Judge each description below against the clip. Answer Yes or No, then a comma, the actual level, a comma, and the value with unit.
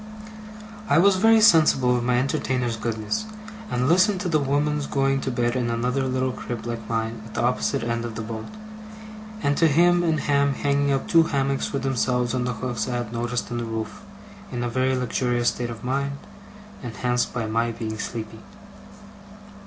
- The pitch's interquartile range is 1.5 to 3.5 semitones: Yes, average, 3.1 semitones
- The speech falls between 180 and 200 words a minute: Yes, average, 185 wpm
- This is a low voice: Yes, low, 125 Hz